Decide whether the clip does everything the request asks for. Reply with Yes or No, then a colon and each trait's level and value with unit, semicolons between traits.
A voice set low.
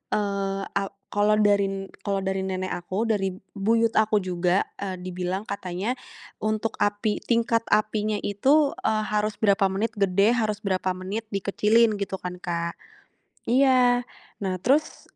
No: high, 205 Hz